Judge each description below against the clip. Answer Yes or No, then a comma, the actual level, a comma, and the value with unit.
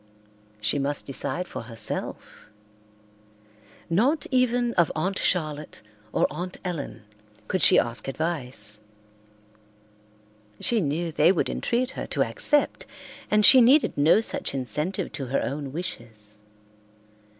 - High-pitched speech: No, medium, 155 Hz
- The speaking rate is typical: No, slow, 120 wpm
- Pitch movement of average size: No, wide, 6.8 semitones